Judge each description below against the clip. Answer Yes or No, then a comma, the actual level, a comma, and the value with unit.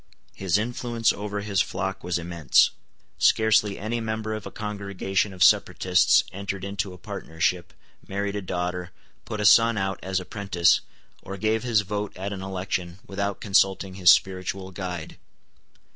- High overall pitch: No, very low, 95 Hz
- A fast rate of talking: No, average, 150 wpm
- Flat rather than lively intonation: Yes, narrow, 2.3 semitones